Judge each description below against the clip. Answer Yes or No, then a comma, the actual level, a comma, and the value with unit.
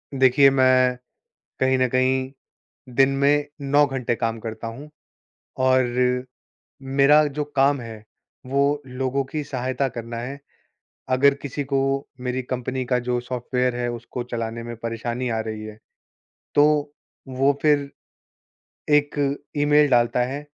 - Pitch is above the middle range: No, low, 130 Hz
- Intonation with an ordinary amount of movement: No, narrow, 2.3 semitones